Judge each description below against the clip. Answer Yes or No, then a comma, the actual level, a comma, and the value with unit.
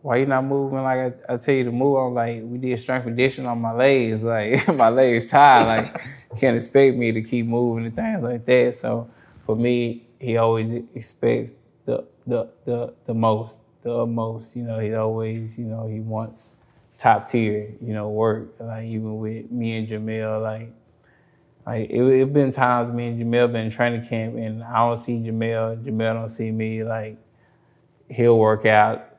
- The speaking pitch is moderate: No, low, 115 Hz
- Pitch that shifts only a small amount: Yes, narrow, 1.7 semitones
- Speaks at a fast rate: No, average, 190 wpm